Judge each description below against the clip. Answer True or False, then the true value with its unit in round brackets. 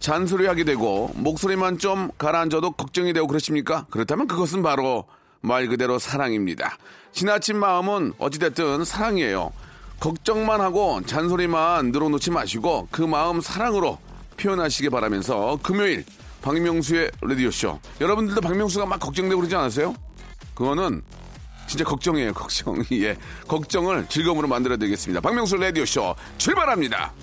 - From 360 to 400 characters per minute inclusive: True (370 characters per minute)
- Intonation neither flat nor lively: False (5.9 semitones)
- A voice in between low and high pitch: True (160 Hz)